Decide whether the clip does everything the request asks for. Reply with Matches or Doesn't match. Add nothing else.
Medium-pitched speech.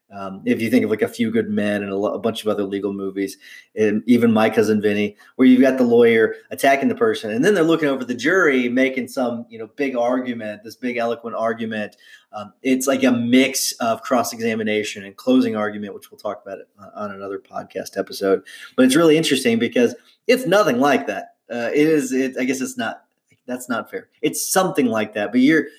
Doesn't match